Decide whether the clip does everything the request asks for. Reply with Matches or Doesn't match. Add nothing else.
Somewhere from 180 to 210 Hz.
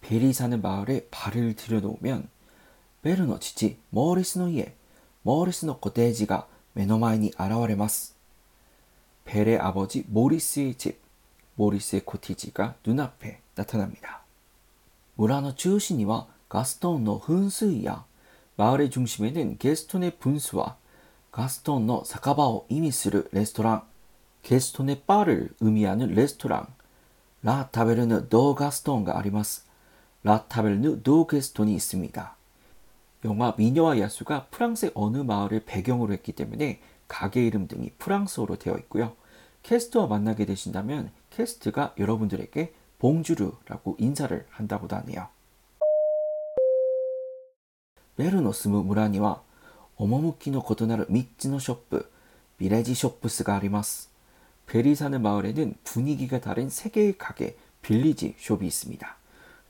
Doesn't match